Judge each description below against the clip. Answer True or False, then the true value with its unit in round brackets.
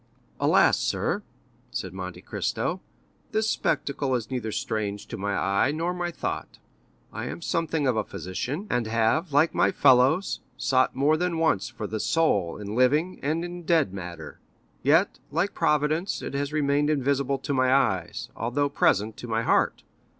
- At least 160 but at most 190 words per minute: True (165 wpm)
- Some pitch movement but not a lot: False (6.1 semitones)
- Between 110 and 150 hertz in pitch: True (140 Hz)